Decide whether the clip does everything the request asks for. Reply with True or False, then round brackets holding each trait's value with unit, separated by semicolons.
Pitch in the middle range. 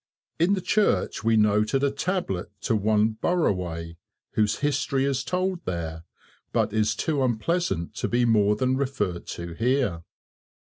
False (115 Hz)